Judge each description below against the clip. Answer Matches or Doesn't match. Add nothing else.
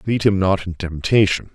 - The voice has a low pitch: Matches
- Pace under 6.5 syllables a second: Matches